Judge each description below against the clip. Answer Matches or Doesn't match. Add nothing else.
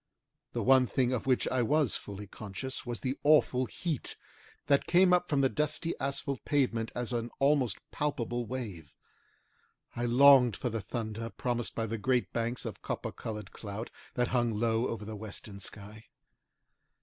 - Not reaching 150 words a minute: Doesn't match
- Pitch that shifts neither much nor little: Matches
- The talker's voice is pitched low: Matches